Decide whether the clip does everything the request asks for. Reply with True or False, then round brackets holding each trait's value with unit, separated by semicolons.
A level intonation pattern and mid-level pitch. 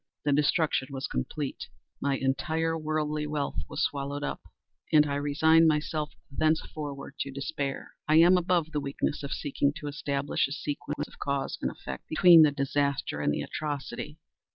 True (1.9 semitones; 145 Hz)